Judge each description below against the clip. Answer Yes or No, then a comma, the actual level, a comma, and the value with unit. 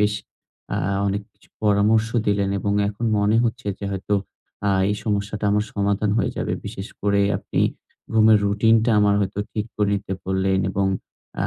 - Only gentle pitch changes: Yes, narrow, 1.0 semitones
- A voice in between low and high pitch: No, low, 105 Hz